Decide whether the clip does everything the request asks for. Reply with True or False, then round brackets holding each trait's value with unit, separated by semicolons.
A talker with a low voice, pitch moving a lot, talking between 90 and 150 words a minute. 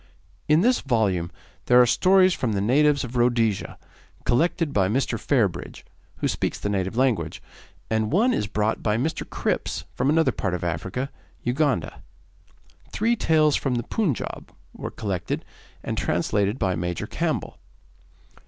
True (120 Hz; 6.6 semitones; 145 wpm)